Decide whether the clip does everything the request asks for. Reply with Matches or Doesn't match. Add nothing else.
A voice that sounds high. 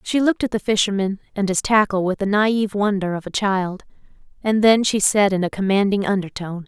Matches